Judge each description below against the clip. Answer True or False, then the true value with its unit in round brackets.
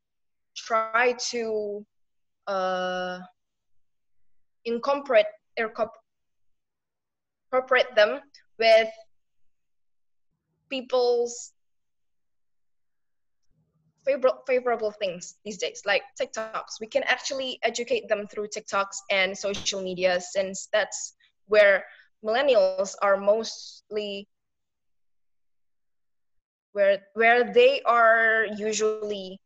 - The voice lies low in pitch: False (215 Hz)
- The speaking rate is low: True (70 wpm)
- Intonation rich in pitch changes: False (4.4 semitones)